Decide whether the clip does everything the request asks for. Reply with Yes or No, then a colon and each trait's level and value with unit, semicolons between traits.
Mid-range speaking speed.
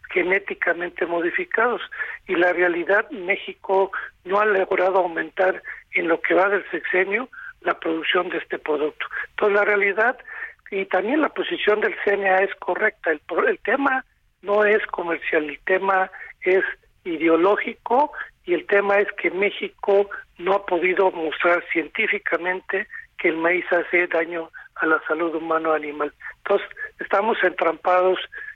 Yes: average, 140 wpm